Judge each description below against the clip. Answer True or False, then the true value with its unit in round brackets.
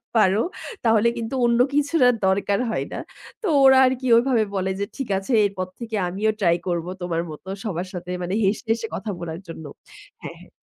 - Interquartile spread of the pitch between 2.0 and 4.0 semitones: False (4.5 semitones)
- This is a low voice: False (205 Hz)